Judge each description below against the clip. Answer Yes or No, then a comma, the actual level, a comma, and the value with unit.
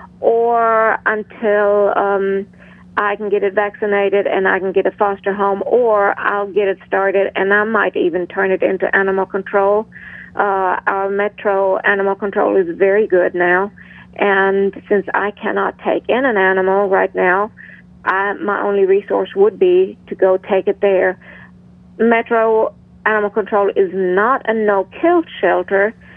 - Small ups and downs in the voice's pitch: Yes, narrow, 1.5 semitones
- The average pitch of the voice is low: No, high, 200 Hz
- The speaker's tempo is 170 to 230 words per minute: No, average, 155 wpm